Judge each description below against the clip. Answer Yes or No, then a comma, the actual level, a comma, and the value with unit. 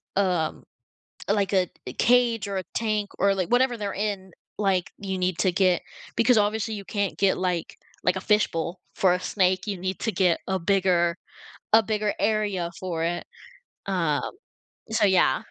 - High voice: Yes, high, 195 Hz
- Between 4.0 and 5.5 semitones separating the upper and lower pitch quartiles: No, narrow, 2.5 semitones